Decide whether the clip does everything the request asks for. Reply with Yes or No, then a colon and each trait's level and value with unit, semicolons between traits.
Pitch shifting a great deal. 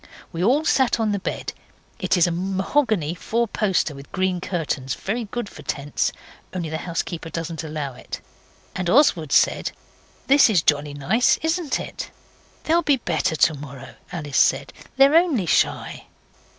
Yes: wide, 7.3 semitones